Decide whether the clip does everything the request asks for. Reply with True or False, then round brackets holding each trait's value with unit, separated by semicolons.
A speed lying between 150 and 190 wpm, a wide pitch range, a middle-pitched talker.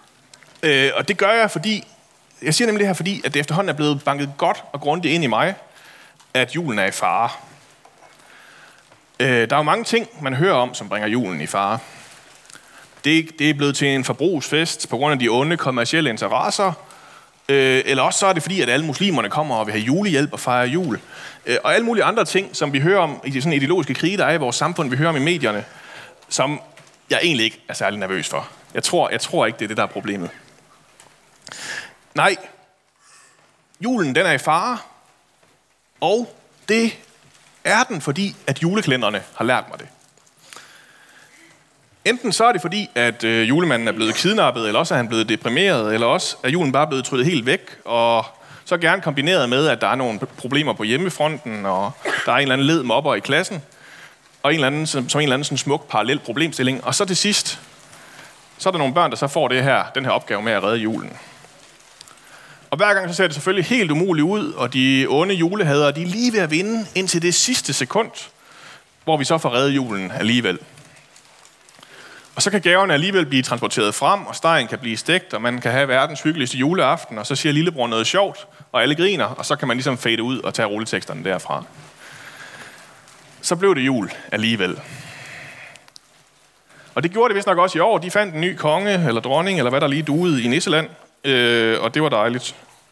False (205 wpm; 6.2 semitones; 150 Hz)